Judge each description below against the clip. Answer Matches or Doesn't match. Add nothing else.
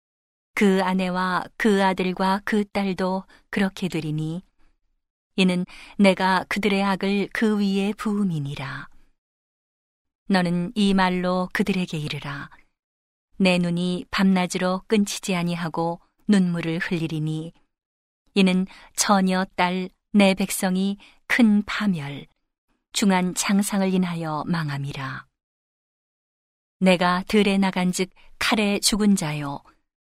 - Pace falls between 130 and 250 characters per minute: Matches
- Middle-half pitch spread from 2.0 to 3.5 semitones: Matches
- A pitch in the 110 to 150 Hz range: Doesn't match